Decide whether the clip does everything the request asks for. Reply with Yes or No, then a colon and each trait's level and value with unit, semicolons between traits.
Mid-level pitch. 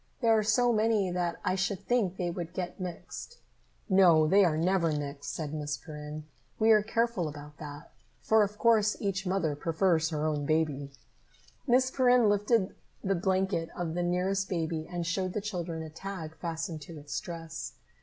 Yes: medium, 175 Hz